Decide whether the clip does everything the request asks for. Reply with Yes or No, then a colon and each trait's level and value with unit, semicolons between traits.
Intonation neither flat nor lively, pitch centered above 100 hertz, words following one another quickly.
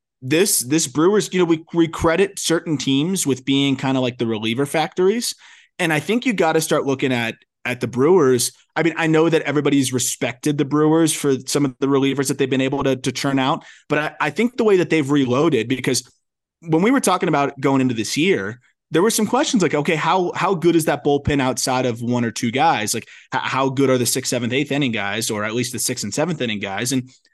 Yes: average, 4.2 semitones; medium, 140 Hz; fast, 235 wpm